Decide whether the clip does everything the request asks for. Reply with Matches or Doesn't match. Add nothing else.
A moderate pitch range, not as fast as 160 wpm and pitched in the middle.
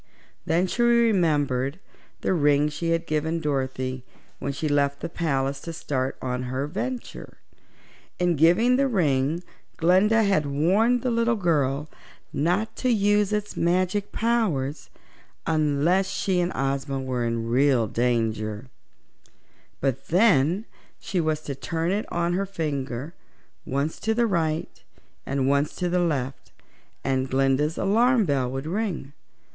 Doesn't match